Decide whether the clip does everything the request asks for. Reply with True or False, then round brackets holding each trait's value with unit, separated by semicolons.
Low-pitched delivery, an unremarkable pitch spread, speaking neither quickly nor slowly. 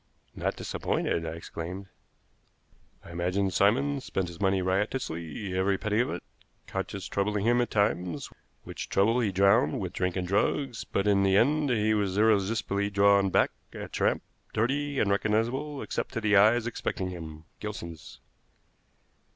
True (100 Hz; 3.2 semitones; 150 wpm)